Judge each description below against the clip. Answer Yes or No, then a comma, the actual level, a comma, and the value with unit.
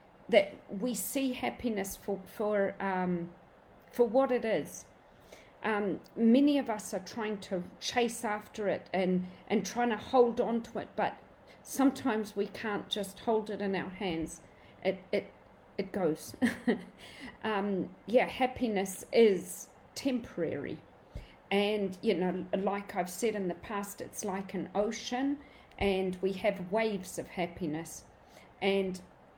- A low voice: No, high, 205 Hz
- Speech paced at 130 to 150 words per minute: Yes, average, 140 wpm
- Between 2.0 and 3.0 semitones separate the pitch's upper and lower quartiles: No, average, 3.4 semitones